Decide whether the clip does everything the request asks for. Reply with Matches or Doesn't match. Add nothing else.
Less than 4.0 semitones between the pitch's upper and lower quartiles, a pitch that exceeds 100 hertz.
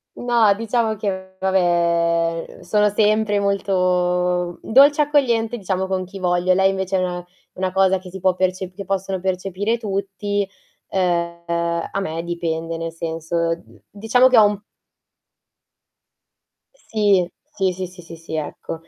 Matches